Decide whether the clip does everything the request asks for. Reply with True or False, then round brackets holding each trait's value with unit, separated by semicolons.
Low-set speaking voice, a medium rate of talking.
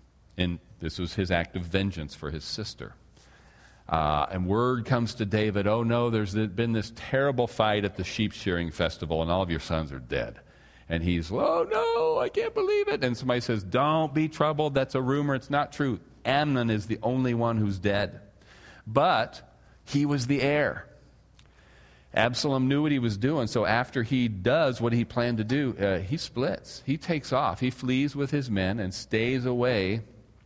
True (120 Hz; 190 wpm)